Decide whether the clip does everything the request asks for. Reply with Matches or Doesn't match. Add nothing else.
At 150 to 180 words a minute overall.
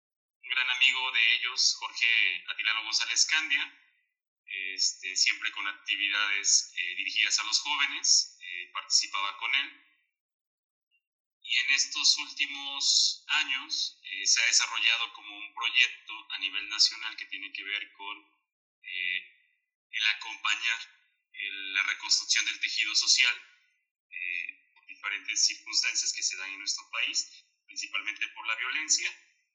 Doesn't match